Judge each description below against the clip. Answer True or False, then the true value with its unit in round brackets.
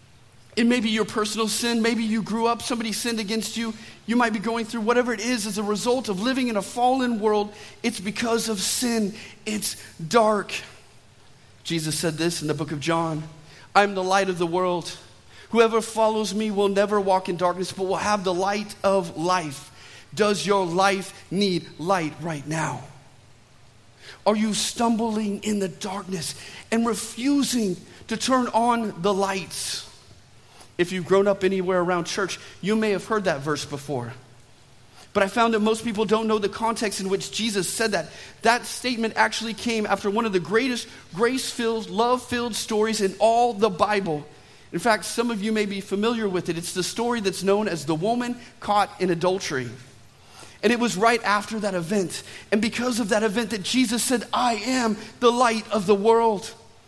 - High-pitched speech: True (205 Hz)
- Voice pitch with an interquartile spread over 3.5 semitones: True (4.3 semitones)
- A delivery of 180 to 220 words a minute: True (185 wpm)